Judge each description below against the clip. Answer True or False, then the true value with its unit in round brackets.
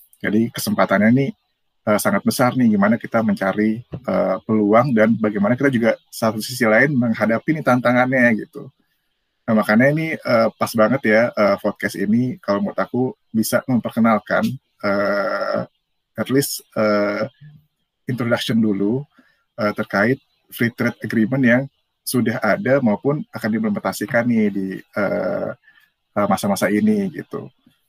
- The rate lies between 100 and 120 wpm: False (135 wpm)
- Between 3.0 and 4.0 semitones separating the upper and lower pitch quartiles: True (3.4 semitones)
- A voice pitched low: True (115 Hz)